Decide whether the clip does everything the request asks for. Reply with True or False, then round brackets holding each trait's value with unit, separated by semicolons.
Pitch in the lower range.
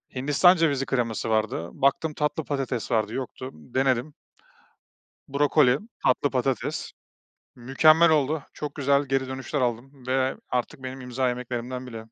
True (130 Hz)